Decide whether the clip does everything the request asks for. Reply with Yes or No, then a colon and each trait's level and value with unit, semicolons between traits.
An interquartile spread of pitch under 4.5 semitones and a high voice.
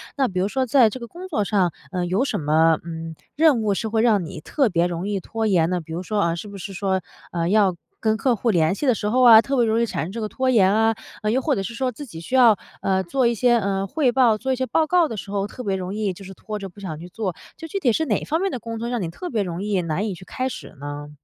No: average, 4.9 semitones; high, 210 Hz